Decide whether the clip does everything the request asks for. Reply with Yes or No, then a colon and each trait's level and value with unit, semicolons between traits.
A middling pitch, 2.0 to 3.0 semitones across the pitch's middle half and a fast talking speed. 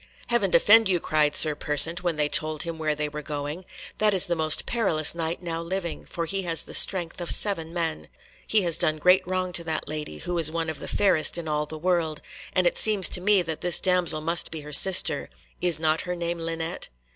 Yes: medium, 165 Hz; narrow, 2.6 semitones; fast, 225 wpm